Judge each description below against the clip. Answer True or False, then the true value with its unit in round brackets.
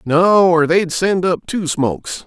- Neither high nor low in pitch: True (170 Hz)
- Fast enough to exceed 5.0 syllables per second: False (3.7 syllables/s)